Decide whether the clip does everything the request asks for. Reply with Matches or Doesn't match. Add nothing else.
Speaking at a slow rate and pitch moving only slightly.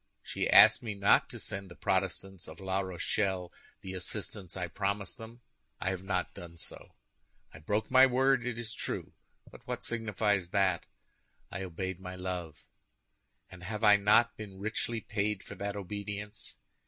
Doesn't match